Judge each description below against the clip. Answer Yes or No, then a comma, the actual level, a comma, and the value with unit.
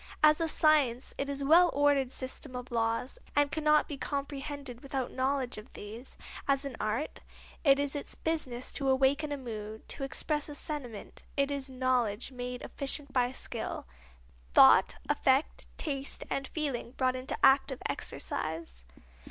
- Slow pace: No, average, 155 wpm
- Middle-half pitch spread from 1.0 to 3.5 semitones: Yes, narrow, 2.5 semitones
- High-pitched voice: Yes, very high, 270 Hz